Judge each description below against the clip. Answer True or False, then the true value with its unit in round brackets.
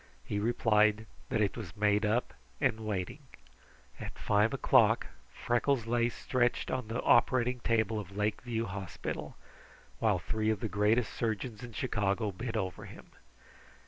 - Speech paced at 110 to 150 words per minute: True (145 wpm)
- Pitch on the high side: False (110 Hz)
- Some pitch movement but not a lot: False (2.3 semitones)